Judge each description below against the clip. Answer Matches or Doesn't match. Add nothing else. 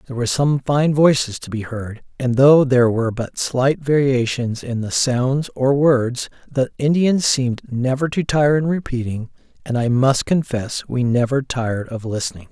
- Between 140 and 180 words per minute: Matches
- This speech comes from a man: Matches